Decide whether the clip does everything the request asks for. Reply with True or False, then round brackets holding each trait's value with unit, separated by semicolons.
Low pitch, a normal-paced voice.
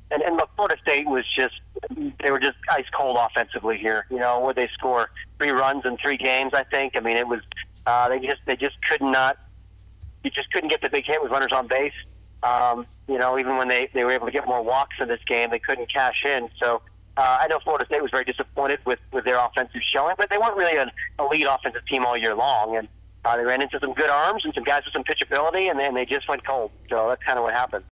False (130 Hz; 260 wpm)